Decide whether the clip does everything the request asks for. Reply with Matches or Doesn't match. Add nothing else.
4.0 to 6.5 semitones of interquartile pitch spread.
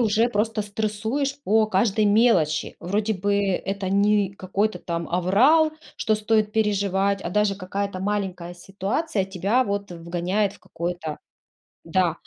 Doesn't match